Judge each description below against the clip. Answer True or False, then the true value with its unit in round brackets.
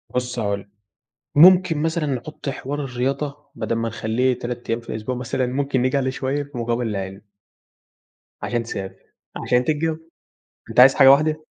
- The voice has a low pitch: True (130 Hz)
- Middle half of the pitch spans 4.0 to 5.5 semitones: False (3.5 semitones)